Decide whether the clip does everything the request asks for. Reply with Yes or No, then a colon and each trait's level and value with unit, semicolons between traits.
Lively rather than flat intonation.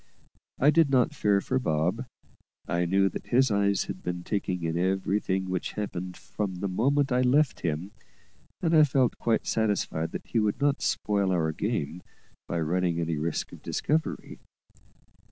Yes: wide, 6.1 semitones